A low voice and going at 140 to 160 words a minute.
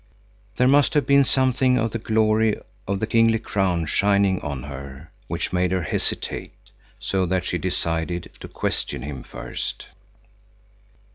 Yes: low, 100 Hz; average, 145 wpm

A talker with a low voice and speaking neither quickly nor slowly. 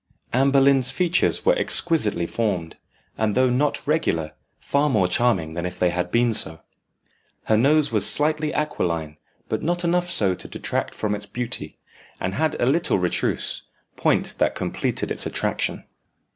Yes: low, 120 Hz; average, 160 wpm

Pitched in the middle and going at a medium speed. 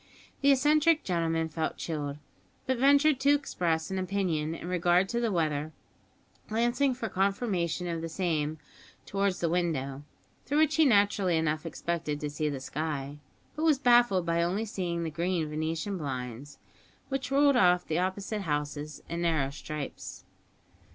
Yes: medium, 175 Hz; average, 155 wpm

